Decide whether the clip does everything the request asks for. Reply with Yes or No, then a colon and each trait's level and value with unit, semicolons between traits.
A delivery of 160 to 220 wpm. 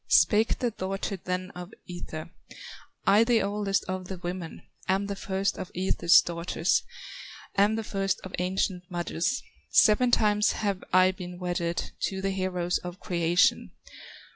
No: average, 145 wpm